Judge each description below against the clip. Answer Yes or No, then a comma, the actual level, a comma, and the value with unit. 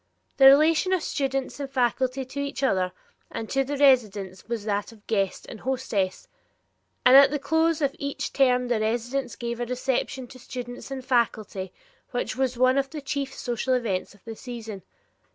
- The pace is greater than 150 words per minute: Yes, average, 180 wpm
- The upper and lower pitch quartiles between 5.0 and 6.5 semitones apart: No, average, 3.2 semitones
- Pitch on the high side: Yes, very high, 255 Hz